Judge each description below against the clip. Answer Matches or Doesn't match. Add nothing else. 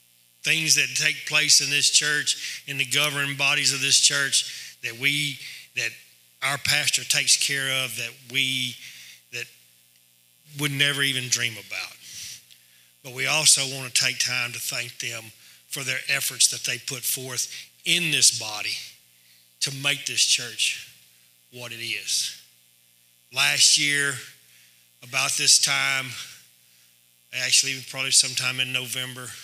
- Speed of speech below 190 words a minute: Matches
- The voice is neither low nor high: Doesn't match